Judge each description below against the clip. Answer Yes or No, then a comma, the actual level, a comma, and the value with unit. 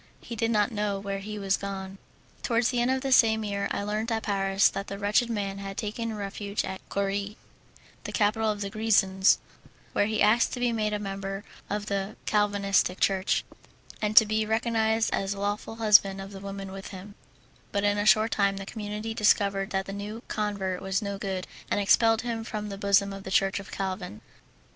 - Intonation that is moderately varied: No, narrow, 1.8 semitones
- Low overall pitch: No, high, 205 Hz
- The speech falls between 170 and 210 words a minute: Yes, average, 200 wpm